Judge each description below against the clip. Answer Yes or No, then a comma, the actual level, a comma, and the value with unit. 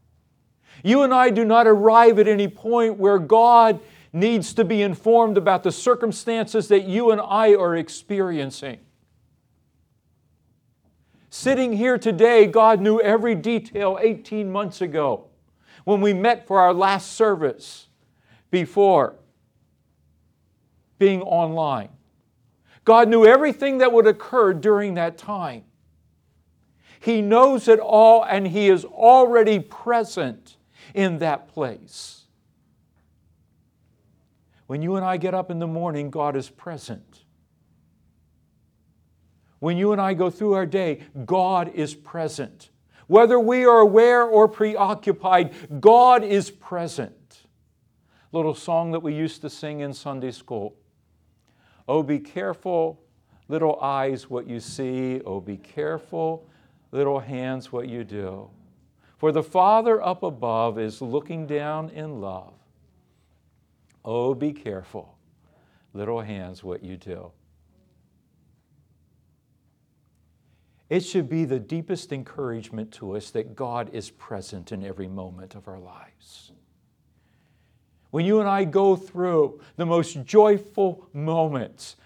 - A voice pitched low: No, medium, 160 Hz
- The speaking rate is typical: No, slow, 125 wpm